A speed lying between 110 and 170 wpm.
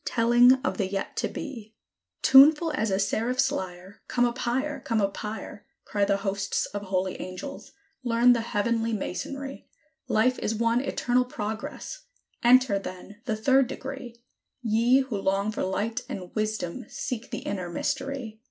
Yes: average, 155 wpm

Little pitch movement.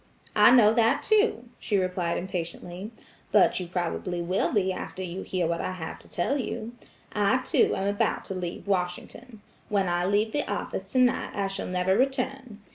No: average, 4.1 semitones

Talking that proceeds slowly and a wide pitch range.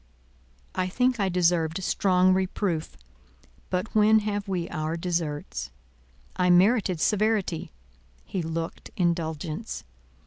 No: slow, 105 wpm; average, 3.5 semitones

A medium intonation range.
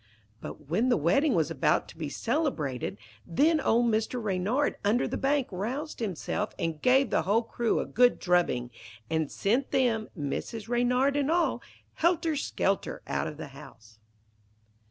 No: wide, 8.3 semitones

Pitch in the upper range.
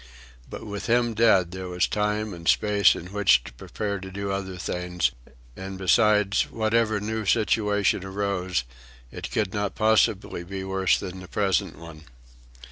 No: low, 100 Hz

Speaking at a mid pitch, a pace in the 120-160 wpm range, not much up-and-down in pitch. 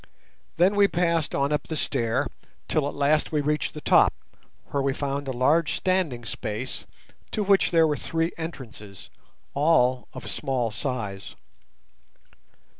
No: medium, 145 Hz; average, 145 wpm; average, 4.3 semitones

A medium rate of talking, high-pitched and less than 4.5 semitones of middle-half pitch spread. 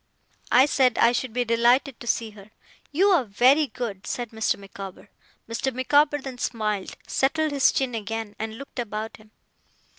Yes: average, 170 wpm; high, 240 Hz; average, 3.5 semitones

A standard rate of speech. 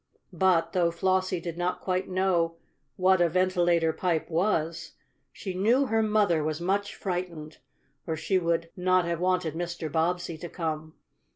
Yes: average, 155 wpm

